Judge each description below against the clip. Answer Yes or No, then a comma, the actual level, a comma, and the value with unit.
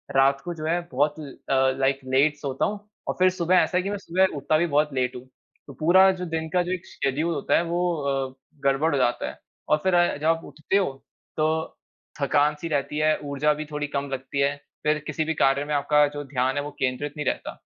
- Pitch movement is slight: No, average, 3.3 semitones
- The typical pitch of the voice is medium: Yes, medium, 150 Hz